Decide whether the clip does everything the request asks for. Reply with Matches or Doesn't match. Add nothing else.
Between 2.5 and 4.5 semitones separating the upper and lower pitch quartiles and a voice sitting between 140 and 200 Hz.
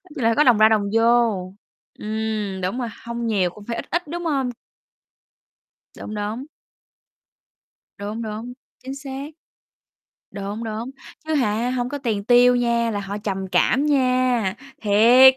Doesn't match